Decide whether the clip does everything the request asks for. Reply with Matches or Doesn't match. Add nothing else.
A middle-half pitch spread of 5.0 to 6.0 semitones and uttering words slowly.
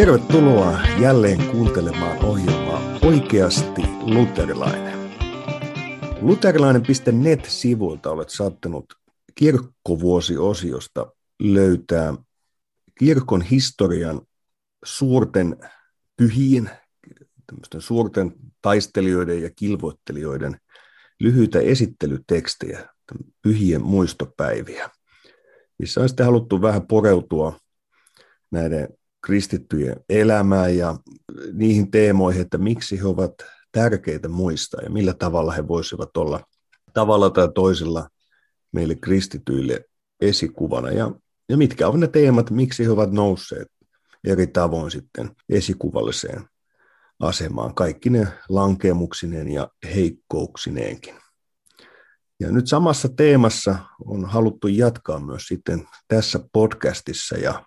Matches